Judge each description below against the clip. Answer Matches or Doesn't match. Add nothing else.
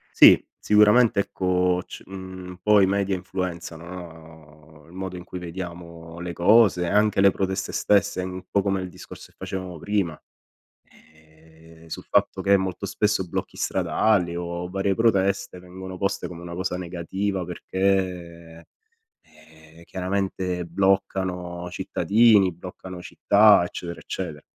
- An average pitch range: Doesn't match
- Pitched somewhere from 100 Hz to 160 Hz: Doesn't match